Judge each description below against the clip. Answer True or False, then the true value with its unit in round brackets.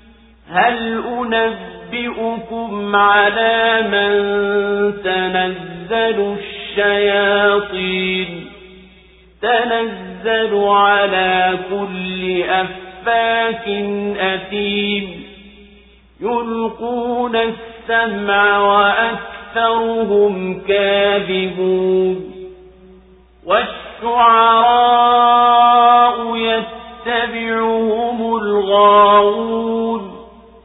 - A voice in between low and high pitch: False (205 Hz)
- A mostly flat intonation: True (2.3 semitones)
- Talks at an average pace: False (35 wpm)